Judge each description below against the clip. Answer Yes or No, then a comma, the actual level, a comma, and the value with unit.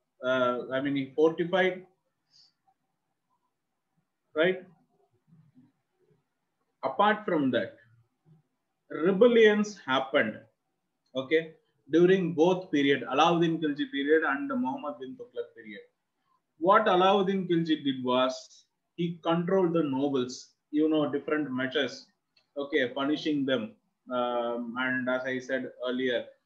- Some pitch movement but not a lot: No, wide, 5.9 semitones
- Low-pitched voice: No, medium, 155 Hz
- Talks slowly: Yes, slow, 100 wpm